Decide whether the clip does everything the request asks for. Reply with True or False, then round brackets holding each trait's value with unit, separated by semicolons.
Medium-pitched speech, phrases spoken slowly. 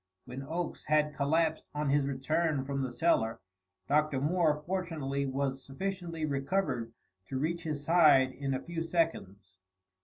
False (145 Hz; 145 wpm)